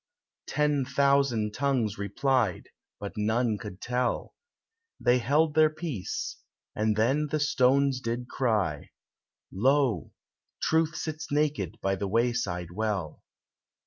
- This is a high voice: No, low, 125 Hz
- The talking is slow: Yes, slow, 115 wpm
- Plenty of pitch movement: No, average, 5.0 semitones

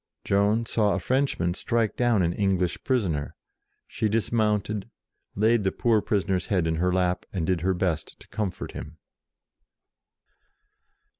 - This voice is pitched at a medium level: No, low, 100 Hz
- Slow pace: No, average, 145 wpm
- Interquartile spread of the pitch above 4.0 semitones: No, average, 3.4 semitones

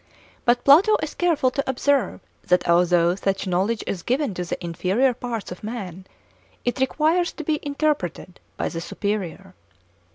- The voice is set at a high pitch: Yes, high, 225 Hz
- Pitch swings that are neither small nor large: No, wide, 7.5 semitones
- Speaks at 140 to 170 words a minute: Yes, average, 155 wpm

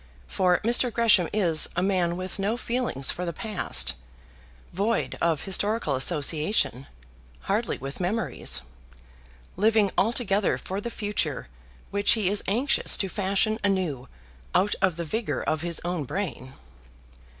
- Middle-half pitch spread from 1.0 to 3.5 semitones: No, average, 4.2 semitones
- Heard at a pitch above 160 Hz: Yes, high, 190 Hz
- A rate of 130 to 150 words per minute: Yes, slow, 135 wpm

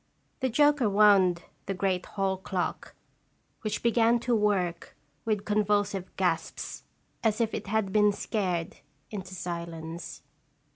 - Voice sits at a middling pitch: No, high, 200 Hz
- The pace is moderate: No, slow, 125 wpm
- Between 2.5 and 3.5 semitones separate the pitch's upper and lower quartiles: Yes, average, 2.8 semitones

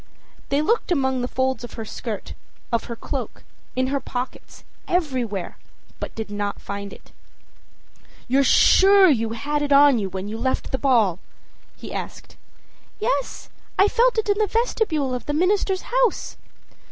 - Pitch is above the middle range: Yes, very high, 265 Hz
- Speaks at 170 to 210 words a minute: No, average, 160 wpm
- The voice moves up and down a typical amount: No, wide, 8.4 semitones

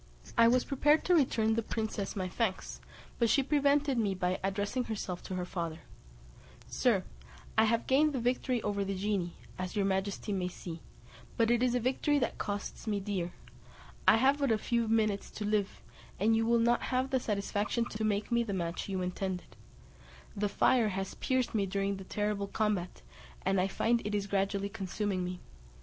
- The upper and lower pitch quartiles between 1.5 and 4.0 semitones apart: Yes, average, 3.4 semitones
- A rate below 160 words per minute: No, average, 185 wpm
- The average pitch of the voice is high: Yes, high, 210 Hz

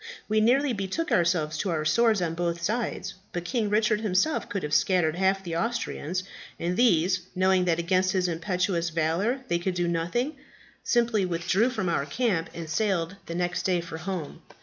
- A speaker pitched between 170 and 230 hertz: Yes, medium, 185 Hz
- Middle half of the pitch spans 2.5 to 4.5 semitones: Yes, average, 4.0 semitones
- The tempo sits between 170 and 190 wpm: Yes, average, 180 wpm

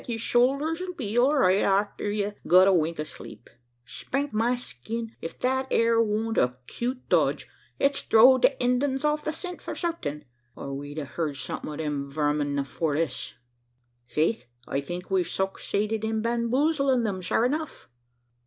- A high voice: Yes, high, 220 Hz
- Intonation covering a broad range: Yes, wide, 8.3 semitones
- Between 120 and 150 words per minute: No, average, 170 wpm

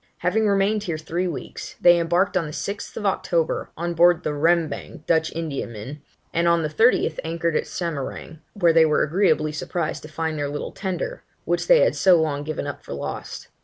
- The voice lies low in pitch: No, medium, 165 Hz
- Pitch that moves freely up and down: No, average, 2.8 semitones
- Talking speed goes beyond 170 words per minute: Yes, average, 190 wpm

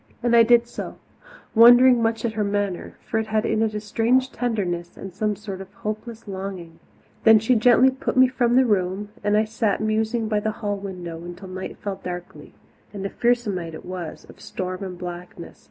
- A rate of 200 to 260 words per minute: Yes, fast, 205 wpm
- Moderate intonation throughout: Yes, average, 3.6 semitones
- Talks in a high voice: Yes, high, 210 Hz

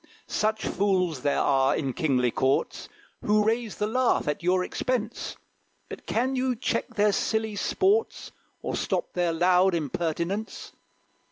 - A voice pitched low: No, high, 195 Hz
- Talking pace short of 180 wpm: Yes, average, 140 wpm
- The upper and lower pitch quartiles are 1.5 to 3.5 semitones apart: No, average, 5.2 semitones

